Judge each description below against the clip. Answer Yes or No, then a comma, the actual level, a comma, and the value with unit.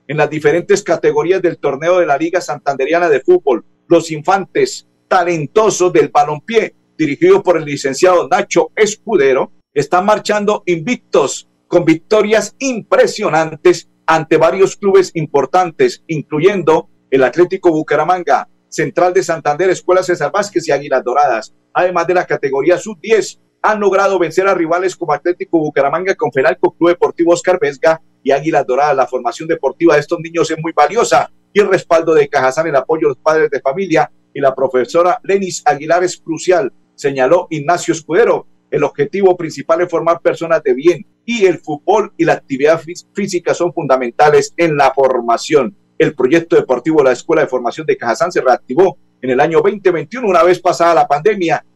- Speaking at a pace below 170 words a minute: Yes, average, 160 wpm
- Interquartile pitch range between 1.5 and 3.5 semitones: No, average, 4.2 semitones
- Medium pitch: Yes, medium, 170 Hz